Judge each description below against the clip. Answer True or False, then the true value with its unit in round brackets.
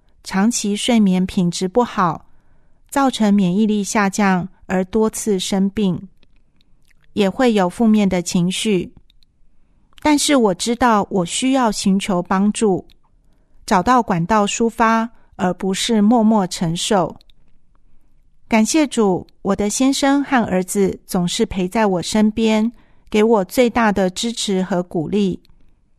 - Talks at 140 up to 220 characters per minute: True (185 characters per minute)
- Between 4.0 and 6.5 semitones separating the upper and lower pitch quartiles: False (3.4 semitones)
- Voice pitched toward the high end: True (205 Hz)